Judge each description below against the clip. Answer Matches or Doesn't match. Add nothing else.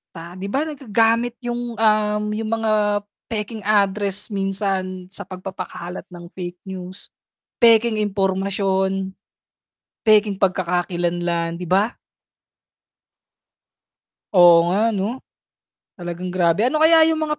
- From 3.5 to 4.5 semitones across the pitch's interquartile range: Doesn't match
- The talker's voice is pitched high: Matches